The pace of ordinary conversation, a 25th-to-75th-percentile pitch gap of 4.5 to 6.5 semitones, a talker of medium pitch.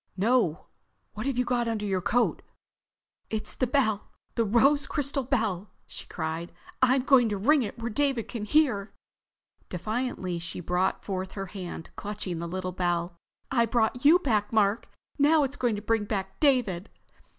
No: average, 165 wpm; average, 5.0 semitones; high, 220 Hz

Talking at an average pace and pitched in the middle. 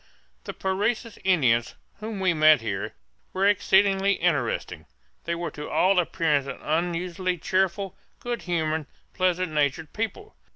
No: slow, 130 wpm; medium, 180 Hz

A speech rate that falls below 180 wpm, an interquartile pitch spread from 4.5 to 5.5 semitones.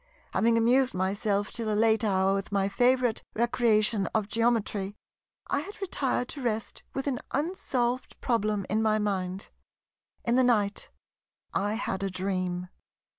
No: average, 145 wpm; average, 3.5 semitones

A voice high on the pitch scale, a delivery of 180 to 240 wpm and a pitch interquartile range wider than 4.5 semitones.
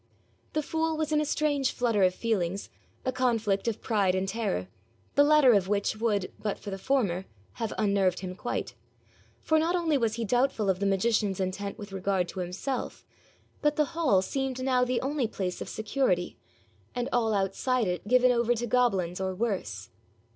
Yes: high, 220 Hz; average, 185 wpm; average, 5.0 semitones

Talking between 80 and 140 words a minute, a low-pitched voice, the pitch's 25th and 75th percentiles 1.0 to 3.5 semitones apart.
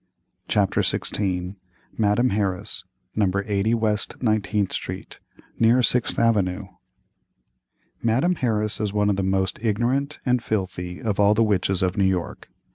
Yes: slow, 135 wpm; low, 105 Hz; average, 2.9 semitones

